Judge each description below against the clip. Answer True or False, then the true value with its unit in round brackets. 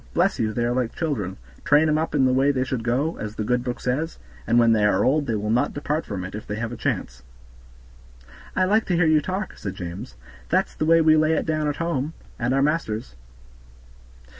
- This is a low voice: True (130 Hz)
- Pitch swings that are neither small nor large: False (5.8 semitones)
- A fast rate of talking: True (235 wpm)